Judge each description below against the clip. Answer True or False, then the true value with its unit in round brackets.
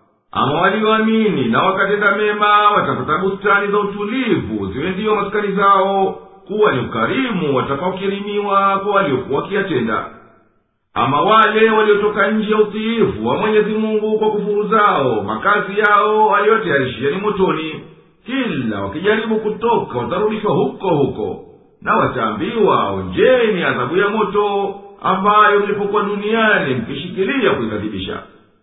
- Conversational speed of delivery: True (110 wpm)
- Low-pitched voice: False (205 Hz)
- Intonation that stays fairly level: True (1.5 semitones)